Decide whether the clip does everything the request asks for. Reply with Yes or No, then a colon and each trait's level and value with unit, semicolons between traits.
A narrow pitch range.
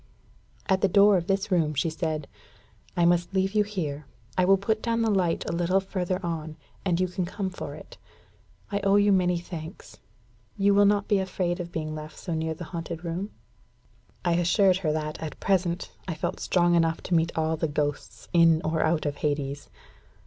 No: average, 3.2 semitones